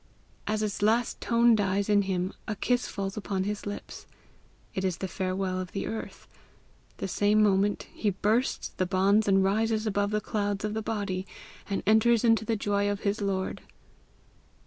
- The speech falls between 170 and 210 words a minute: Yes, average, 175 wpm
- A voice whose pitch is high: Yes, high, 205 Hz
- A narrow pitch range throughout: Yes, narrow, 1.8 semitones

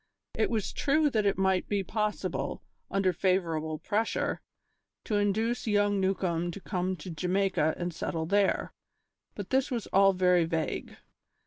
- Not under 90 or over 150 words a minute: Yes, average, 145 wpm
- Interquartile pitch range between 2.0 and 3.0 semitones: Yes, average, 2.7 semitones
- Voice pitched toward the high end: Yes, high, 195 Hz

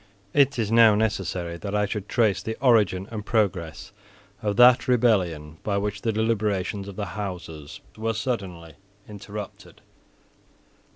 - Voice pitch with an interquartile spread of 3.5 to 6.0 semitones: No, average, 3.1 semitones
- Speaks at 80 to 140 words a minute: Yes, slow, 135 wpm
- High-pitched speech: No, low, 105 Hz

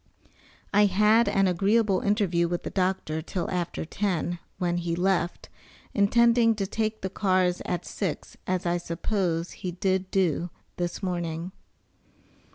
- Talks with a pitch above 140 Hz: Yes, medium, 185 Hz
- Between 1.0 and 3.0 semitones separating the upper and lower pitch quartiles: Yes, narrow, 2.6 semitones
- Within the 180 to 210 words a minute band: No, average, 140 wpm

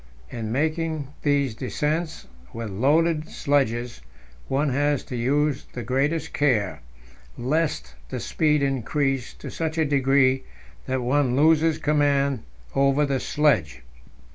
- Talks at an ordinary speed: No, slow, 120 wpm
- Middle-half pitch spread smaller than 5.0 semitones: Yes, average, 2.9 semitones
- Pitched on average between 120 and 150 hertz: Yes, medium, 140 Hz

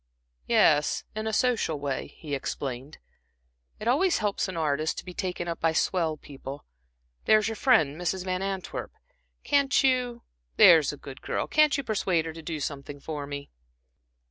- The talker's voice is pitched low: No, medium, 170 Hz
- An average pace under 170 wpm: Yes, average, 160 wpm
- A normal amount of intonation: No, wide, 6.8 semitones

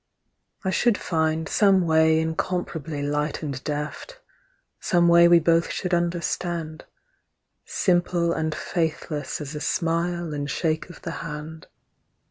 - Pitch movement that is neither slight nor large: No, narrow, 1.9 semitones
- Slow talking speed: Yes, slow, 125 wpm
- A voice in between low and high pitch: Yes, medium, 165 Hz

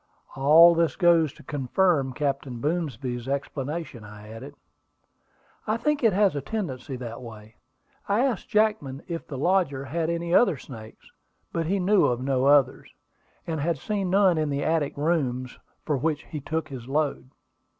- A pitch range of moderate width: Yes, average, 4.6 semitones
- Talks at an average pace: Yes, average, 160 wpm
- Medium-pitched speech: Yes, medium, 150 Hz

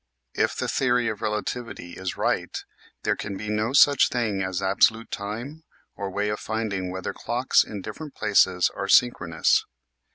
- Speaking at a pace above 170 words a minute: No, average, 160 wpm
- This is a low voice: Yes, low, 105 Hz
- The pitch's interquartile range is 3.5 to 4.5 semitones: Yes, average, 3.8 semitones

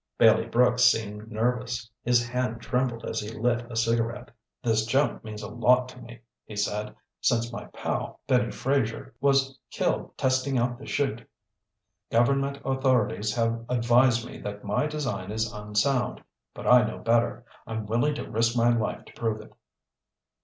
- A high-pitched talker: No, low, 120 Hz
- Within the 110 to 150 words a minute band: No, average, 160 wpm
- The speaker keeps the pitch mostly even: Yes, narrow, 2.1 semitones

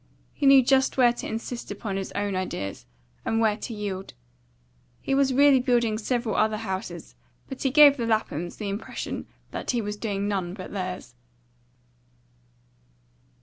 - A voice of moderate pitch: No, high, 220 Hz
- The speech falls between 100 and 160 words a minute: Yes, average, 155 wpm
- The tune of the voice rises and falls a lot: No, average, 4.2 semitones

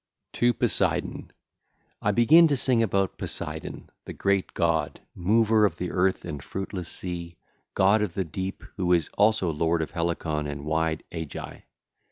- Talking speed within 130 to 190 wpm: Yes, average, 175 wpm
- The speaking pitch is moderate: No, very low, 90 Hz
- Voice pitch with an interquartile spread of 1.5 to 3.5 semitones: No, average, 4.1 semitones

